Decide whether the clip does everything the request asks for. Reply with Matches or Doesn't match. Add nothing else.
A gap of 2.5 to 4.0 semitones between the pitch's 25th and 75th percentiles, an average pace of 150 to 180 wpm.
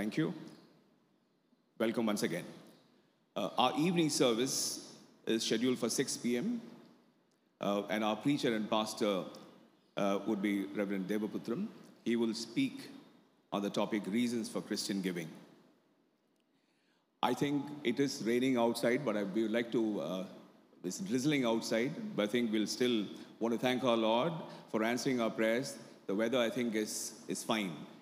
Matches